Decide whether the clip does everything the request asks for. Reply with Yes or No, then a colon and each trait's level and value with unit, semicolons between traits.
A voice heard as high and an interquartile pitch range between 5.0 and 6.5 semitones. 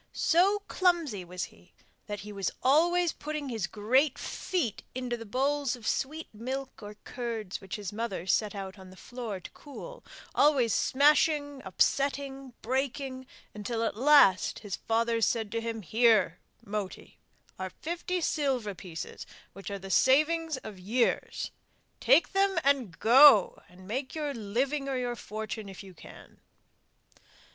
Yes: high, 240 Hz; wide, 5.5 semitones